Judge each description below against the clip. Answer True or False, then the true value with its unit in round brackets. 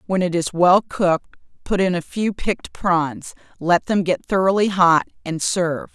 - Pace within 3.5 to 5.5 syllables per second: True (4.7 syllables/s)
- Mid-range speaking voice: True (180 Hz)